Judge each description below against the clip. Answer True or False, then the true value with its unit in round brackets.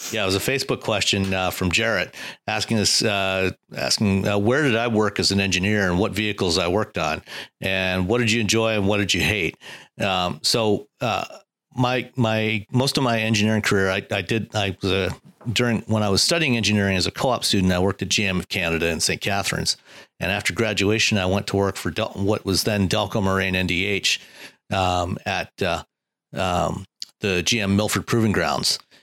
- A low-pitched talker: True (100 Hz)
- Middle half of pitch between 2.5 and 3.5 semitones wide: True (2.8 semitones)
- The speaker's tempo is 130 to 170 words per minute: False (200 wpm)